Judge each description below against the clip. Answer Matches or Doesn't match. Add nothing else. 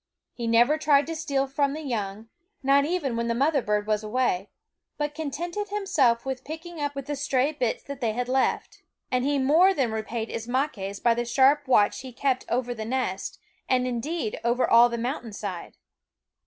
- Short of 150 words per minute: Doesn't match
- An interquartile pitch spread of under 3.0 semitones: Doesn't match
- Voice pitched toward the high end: Matches